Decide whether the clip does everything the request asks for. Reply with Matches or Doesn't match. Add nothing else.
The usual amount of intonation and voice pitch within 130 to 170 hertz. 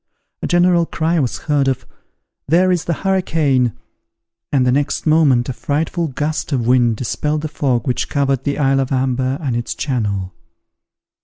Matches